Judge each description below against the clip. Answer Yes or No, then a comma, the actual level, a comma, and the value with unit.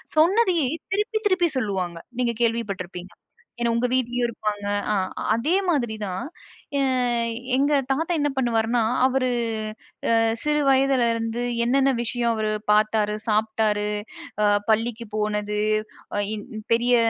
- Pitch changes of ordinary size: Yes, average, 3.9 semitones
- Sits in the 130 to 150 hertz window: No, high, 235 Hz